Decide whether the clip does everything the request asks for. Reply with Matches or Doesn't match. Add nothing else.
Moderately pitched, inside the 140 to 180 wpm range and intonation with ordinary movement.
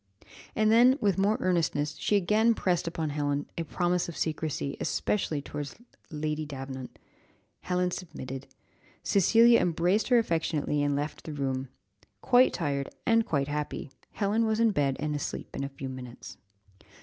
Doesn't match